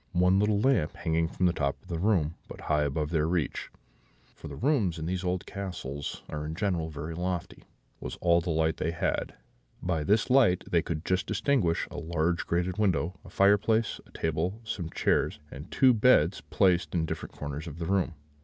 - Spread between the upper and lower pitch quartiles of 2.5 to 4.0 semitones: Yes, average, 3.4 semitones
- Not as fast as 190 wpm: No, average, 195 wpm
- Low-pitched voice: Yes, very low, 85 Hz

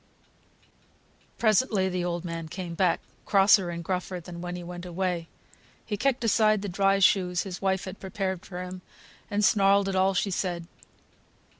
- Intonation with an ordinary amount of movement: No, narrow, 1.9 semitones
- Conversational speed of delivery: Yes, average, 165 wpm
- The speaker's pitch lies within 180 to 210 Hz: Yes, medium, 185 Hz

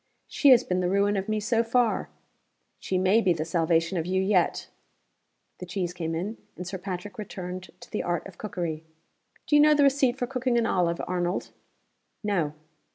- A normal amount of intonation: Yes, average, 4.2 semitones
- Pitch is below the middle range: No, high, 190 Hz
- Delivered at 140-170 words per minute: No, average, 190 wpm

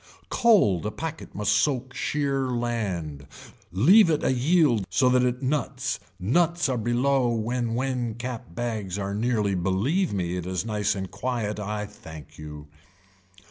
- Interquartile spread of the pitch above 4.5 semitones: Yes, average, 4.9 semitones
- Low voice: Yes, low, 120 Hz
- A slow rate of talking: No, average, 145 wpm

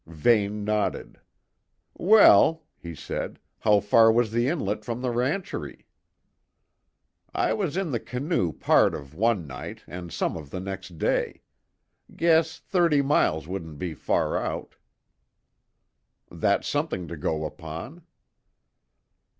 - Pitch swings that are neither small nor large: No, wide, 9.0 semitones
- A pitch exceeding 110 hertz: No, low, 105 Hz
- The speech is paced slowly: Yes, slow, 125 wpm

